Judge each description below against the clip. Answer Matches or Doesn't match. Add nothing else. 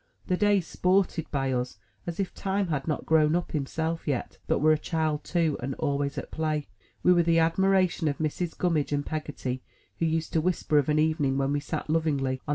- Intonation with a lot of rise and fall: Doesn't match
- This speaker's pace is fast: Matches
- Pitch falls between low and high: Matches